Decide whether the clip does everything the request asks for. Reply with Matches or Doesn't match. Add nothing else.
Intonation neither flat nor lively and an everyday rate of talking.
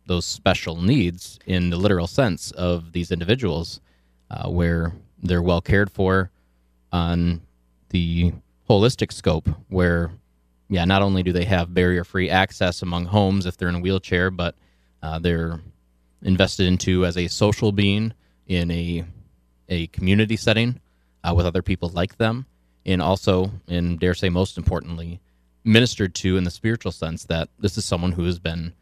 Doesn't match